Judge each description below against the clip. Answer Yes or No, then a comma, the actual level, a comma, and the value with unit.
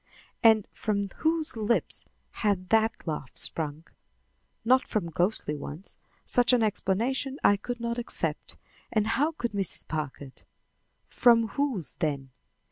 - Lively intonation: Yes, wide, 6.0 semitones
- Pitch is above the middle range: Yes, high, 215 Hz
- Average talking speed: No, slow, 125 wpm